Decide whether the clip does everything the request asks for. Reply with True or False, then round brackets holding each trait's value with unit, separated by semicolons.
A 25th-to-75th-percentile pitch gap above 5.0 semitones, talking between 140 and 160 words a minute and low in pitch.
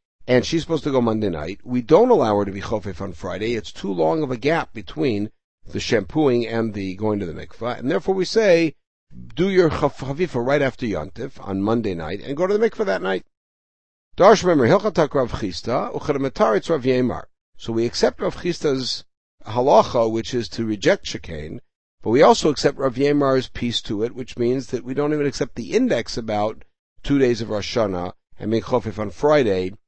False (5.4 semitones; 180 wpm; 125 Hz)